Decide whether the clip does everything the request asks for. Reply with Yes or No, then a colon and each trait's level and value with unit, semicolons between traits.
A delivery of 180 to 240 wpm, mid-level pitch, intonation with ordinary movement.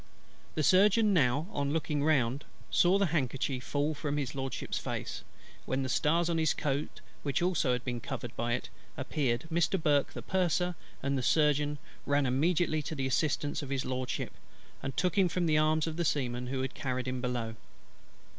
Yes: average, 185 wpm; medium, 145 Hz; average, 3.7 semitones